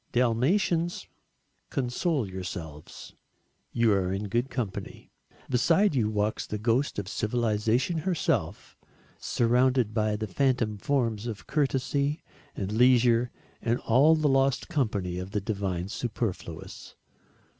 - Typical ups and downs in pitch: Yes, average, 4.4 semitones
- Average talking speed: No, slow, 115 wpm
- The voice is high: No, low, 115 Hz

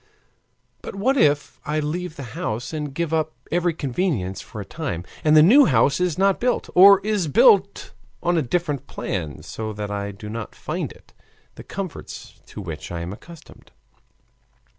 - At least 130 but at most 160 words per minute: No, average, 180 wpm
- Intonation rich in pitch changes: Yes, wide, 8.5 semitones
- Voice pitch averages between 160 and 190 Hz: No, medium, 150 Hz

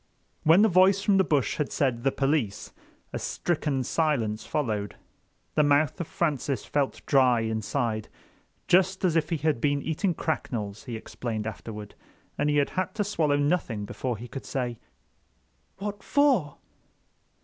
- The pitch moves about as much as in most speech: No, wide, 6.0 semitones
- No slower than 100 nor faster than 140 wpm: No, average, 150 wpm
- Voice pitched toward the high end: No, medium, 145 Hz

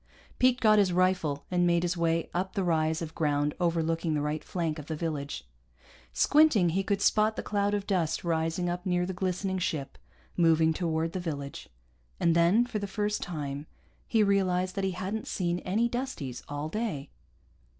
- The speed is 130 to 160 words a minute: No, average, 180 wpm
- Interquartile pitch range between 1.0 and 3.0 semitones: No, average, 3.5 semitones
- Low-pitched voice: No, medium, 175 Hz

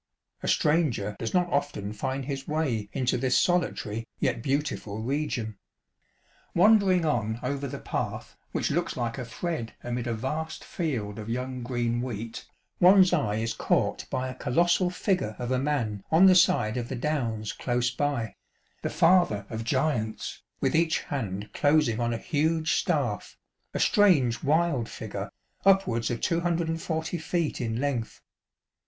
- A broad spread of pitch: Yes, wide, 5.8 semitones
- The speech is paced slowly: No, average, 155 wpm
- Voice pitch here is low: Yes, low, 130 Hz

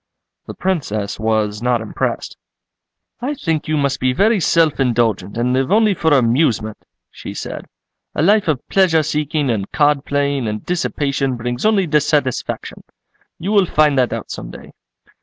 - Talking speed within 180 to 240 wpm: No, average, 160 wpm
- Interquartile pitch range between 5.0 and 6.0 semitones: Yes, wide, 5.4 semitones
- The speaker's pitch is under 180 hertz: Yes, medium, 140 Hz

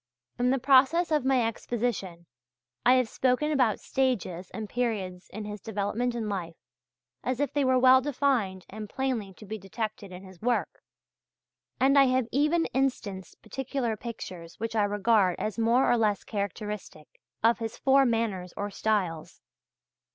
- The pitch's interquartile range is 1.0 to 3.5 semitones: No, average, 4.4 semitones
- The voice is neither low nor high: No, high, 225 Hz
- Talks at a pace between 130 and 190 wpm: Yes, average, 160 wpm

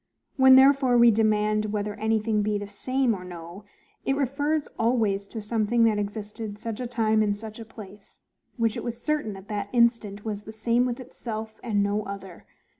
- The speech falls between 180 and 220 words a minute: Yes, average, 190 wpm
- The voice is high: Yes, high, 220 Hz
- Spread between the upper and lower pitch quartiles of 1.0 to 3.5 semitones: Yes, narrow, 2.4 semitones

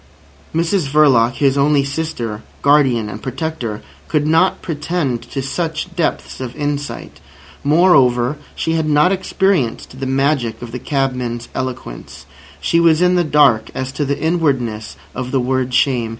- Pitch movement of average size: Yes, average, 4.2 semitones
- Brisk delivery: No, average, 150 wpm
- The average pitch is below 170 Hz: Yes, medium, 140 Hz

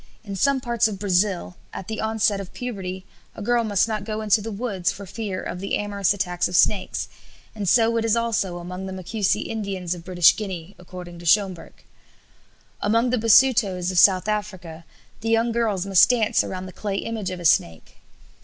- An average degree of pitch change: Yes, average, 3.3 semitones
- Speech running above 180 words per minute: Yes, average, 190 wpm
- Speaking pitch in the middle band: No, high, 200 Hz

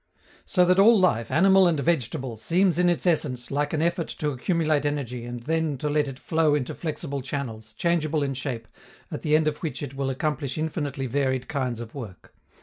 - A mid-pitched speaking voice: Yes, medium, 145 Hz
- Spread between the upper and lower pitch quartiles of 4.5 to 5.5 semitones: No, average, 4.0 semitones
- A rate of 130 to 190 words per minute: No, average, 200 wpm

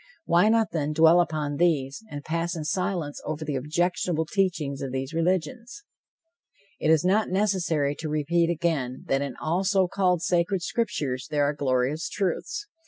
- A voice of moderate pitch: Yes, medium, 165 Hz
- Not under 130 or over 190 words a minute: Yes, average, 165 wpm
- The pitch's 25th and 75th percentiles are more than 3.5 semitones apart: Yes, average, 4.0 semitones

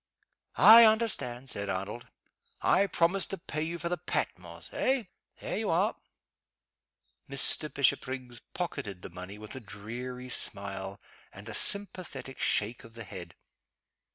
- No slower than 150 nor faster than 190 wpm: No, slow, 135 wpm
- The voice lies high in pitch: No, low, 125 Hz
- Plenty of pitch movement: Yes, wide, 8.6 semitones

